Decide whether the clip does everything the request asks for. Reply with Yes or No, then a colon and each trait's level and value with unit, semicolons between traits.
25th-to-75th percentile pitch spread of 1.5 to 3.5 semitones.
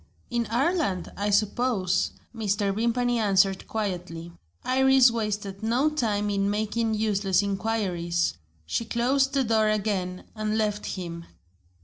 Yes: average, 3.1 semitones